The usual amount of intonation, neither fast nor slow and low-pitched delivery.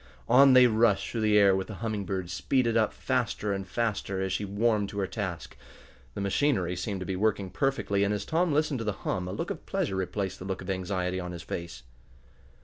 No: average, 3.2 semitones; fast, 225 wpm; low, 100 Hz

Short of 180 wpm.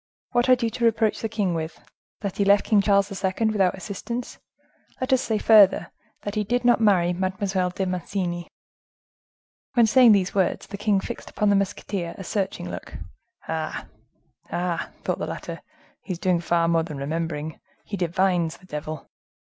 Yes: average, 165 wpm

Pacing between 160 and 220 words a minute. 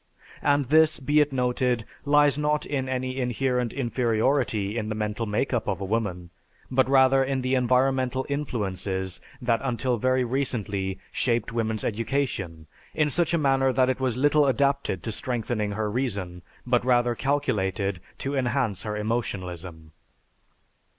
No: average, 145 wpm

